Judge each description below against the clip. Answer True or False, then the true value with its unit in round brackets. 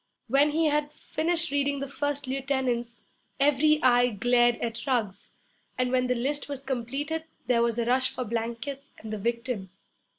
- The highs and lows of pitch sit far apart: False (3.3 semitones)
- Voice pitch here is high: True (255 Hz)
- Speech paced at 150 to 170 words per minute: True (165 wpm)